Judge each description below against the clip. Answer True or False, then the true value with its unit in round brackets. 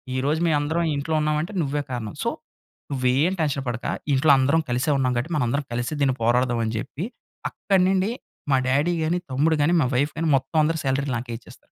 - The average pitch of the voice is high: False (140 Hz)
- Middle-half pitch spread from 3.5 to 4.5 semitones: True (3.8 semitones)